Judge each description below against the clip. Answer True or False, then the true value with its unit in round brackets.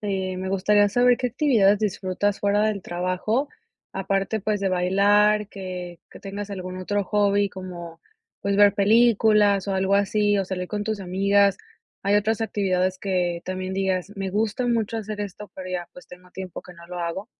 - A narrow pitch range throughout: True (2.0 semitones)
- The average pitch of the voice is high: True (195 Hz)